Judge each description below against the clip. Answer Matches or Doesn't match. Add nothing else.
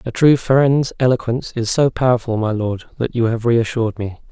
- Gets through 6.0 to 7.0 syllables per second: Doesn't match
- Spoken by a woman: Doesn't match